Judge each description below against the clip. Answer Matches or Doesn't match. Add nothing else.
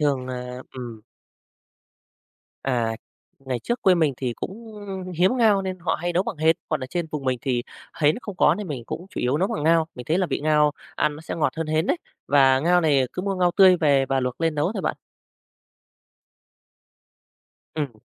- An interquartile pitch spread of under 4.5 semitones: Doesn't match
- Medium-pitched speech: Matches